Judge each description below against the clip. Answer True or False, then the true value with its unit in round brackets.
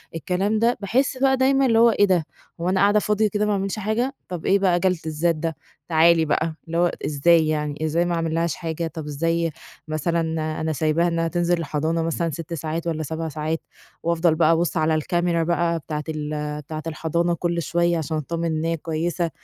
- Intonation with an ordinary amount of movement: False (1.9 semitones)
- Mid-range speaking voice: True (165 Hz)